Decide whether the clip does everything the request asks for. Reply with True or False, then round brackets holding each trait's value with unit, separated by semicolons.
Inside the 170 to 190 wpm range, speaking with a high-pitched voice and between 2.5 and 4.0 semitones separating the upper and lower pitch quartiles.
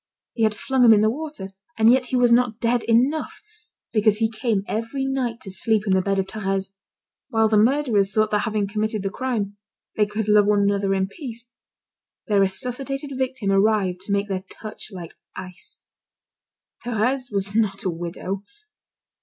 True (180 wpm; 215 Hz; 3.5 semitones)